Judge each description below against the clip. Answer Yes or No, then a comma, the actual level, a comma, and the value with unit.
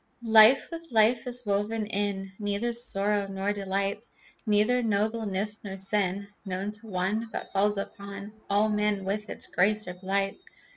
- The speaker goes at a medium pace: Yes, average, 150 wpm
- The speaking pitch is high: Yes, high, 205 Hz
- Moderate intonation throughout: No, narrow, 1.7 semitones